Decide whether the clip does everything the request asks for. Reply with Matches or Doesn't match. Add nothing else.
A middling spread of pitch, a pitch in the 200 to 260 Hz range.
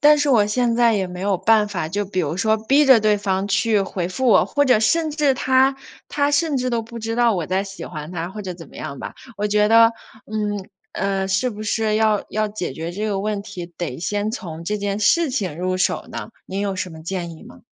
Matches